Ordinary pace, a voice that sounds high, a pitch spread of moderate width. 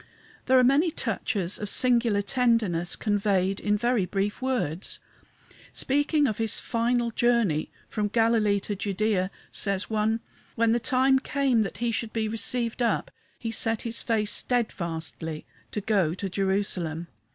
Yes: average, 145 wpm; high, 220 Hz; average, 3.3 semitones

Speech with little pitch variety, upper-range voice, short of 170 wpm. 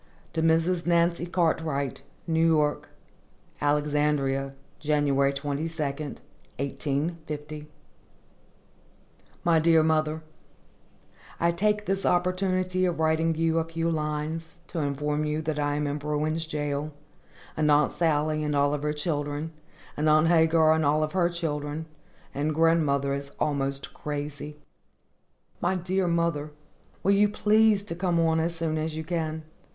No: narrow, 2.1 semitones; medium, 155 Hz; slow, 135 wpm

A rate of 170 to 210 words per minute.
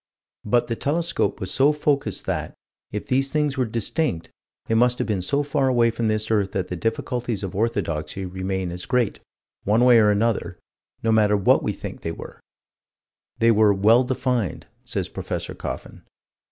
Yes: average, 175 wpm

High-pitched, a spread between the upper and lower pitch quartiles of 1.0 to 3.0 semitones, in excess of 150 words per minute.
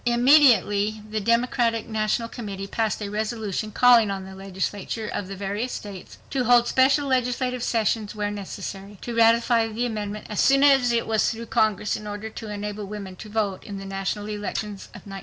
Yes: high, 215 Hz; narrow, 2.6 semitones; average, 185 wpm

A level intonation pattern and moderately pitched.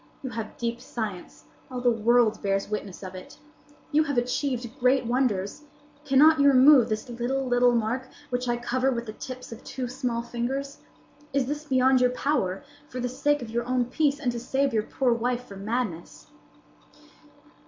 No: narrow, 2.3 semitones; high, 245 Hz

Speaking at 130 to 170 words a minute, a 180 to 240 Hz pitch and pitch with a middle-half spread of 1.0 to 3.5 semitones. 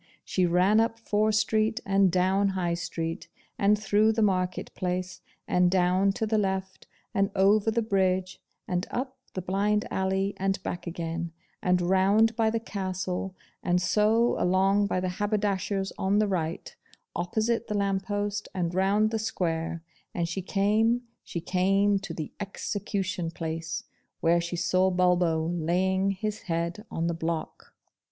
Yes: average, 155 wpm; high, 190 Hz; narrow, 2.6 semitones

